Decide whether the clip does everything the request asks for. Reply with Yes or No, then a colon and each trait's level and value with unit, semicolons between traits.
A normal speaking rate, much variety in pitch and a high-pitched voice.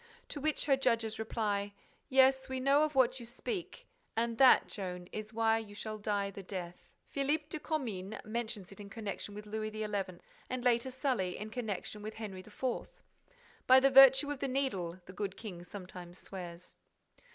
No: average, 175 wpm; average, 4.7 semitones; high, 220 Hz